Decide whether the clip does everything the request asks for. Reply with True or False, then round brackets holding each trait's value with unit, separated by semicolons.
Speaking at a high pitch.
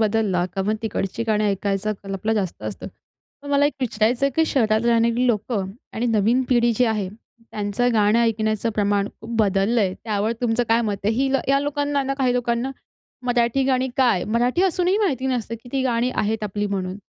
True (230 Hz)